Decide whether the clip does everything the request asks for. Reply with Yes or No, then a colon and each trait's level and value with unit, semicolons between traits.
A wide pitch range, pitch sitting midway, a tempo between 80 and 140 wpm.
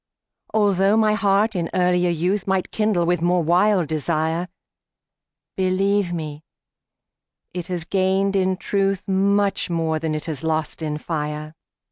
No: average, 3.4 semitones; medium, 180 Hz; slow, 135 wpm